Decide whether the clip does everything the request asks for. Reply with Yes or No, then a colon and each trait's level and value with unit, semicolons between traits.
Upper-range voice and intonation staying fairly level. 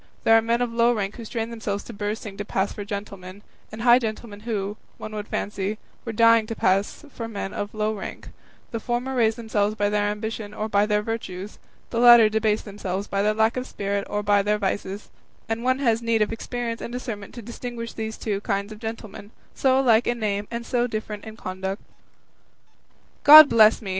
Yes: high, 215 Hz; narrow, 2.2 semitones